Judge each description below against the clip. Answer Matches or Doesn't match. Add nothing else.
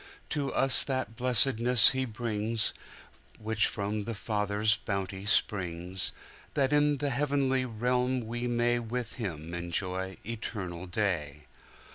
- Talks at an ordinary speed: Doesn't match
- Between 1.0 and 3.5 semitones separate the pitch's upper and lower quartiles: Doesn't match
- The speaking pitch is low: Matches